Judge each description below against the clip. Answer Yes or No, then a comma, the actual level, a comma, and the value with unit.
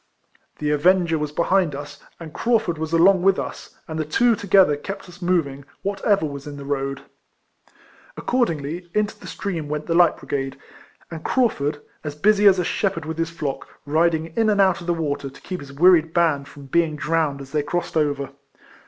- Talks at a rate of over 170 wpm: Yes, average, 190 wpm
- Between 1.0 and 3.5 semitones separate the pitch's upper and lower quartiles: No, average, 4.0 semitones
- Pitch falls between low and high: Yes, medium, 165 Hz